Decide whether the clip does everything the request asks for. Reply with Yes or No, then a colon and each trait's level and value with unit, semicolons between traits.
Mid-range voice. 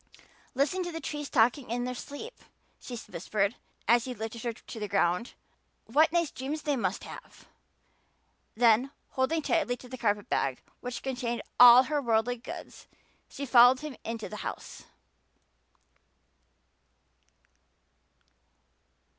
No: high, 245 Hz